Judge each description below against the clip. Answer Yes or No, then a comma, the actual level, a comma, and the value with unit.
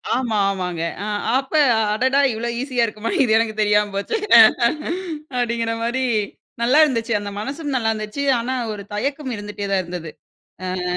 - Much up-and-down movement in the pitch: No, average, 3.8 semitones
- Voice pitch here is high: Yes, high, 230 Hz